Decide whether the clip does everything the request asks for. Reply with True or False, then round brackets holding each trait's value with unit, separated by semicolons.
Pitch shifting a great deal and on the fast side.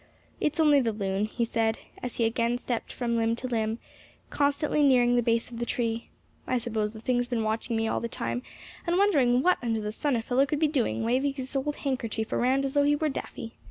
False (3.3 semitones; 230 wpm)